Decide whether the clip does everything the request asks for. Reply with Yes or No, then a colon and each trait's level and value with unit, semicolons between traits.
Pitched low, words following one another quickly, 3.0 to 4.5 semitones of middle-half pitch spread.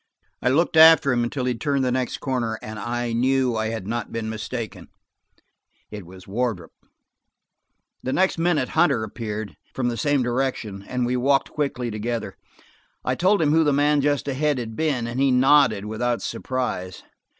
No: low, 125 Hz; average, 170 wpm; average, 3.8 semitones